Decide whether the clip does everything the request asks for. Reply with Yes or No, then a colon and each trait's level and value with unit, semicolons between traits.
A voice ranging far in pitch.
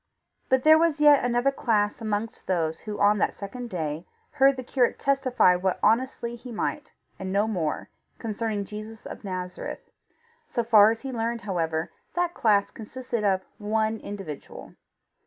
No: average, 3.8 semitones